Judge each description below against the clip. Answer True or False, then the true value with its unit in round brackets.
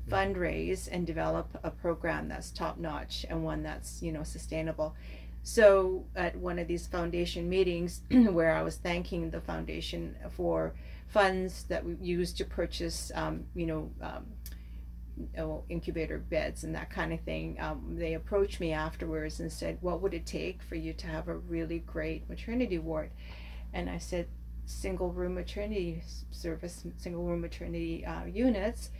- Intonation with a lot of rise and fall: False (2.7 semitones)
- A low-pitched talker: False (165 Hz)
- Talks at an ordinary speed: True (160 wpm)